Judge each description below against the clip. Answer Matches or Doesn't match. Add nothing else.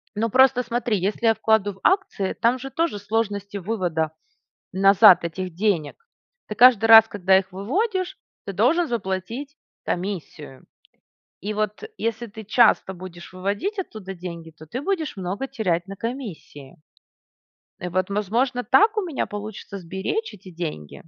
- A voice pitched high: Matches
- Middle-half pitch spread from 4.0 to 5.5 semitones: Matches